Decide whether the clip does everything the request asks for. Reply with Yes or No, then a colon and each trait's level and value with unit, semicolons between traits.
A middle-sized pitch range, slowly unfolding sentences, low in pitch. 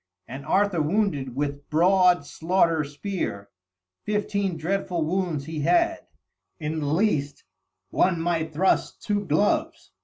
No: average, 4.6 semitones; slow, 120 wpm; medium, 165 Hz